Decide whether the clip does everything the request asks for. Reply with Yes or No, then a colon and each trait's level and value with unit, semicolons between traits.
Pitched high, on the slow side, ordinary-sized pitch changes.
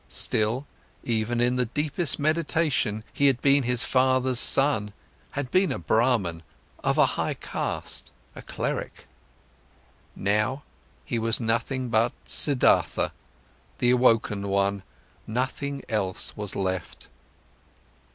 No: low, 120 Hz; slow, 115 wpm; average, 4.0 semitones